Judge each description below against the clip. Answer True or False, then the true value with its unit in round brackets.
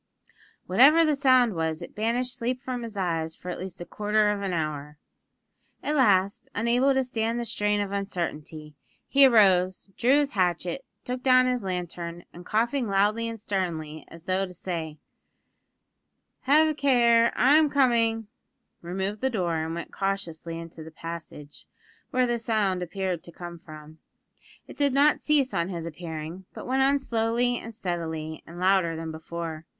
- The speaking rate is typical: True (165 wpm)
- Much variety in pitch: True (6.4 semitones)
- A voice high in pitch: True (195 Hz)